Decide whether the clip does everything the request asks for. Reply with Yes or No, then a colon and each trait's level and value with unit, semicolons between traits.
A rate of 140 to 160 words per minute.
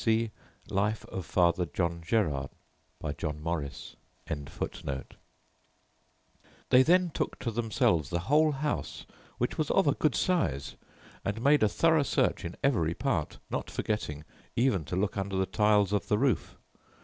Yes: average, 150 wpm